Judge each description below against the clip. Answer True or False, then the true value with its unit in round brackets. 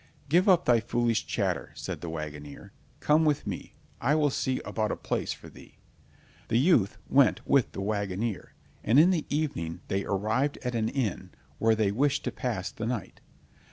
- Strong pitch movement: True (5.9 semitones)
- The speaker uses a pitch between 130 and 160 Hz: False (115 Hz)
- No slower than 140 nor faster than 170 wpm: False (185 wpm)